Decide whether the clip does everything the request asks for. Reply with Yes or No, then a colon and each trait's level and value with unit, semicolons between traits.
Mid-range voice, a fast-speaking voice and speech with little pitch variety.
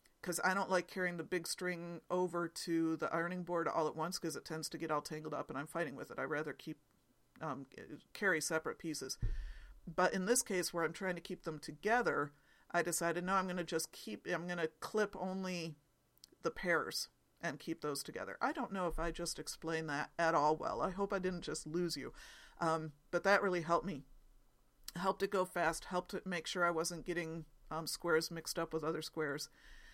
Yes: medium, 170 Hz; fast, 220 wpm; narrow, 2.3 semitones